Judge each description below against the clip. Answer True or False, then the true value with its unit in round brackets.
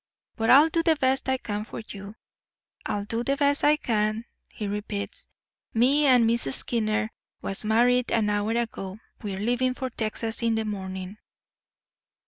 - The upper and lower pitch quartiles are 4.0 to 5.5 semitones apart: False (3.5 semitones)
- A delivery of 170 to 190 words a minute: False (155 wpm)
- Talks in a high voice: True (225 Hz)